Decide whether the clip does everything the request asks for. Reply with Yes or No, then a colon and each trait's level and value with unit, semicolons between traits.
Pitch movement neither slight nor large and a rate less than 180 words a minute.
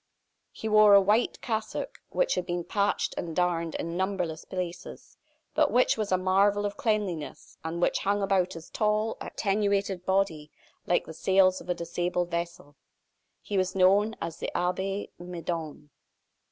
Yes: average, 3.0 semitones; average, 155 wpm